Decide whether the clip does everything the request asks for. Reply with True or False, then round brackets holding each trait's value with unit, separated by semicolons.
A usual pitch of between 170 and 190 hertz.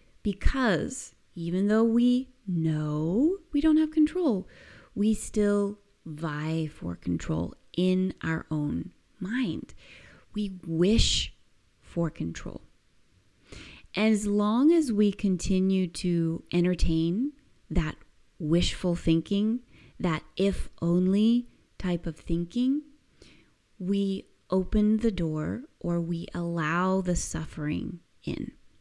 True (185 Hz)